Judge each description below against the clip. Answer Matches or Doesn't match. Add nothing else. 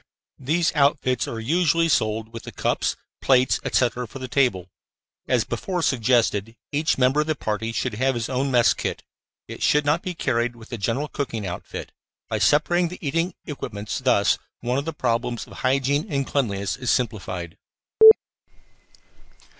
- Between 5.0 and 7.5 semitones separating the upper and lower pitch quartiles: Doesn't match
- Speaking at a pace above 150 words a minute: Matches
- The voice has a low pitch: Matches